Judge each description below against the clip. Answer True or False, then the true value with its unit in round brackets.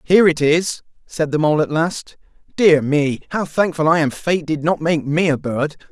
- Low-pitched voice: False (155 Hz)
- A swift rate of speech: True (215 wpm)